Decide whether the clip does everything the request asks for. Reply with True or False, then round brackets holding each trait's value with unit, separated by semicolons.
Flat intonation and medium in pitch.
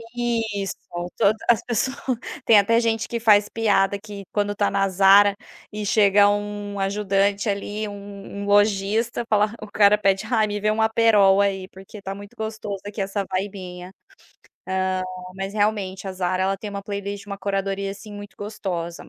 False (1.4 semitones; 205 Hz)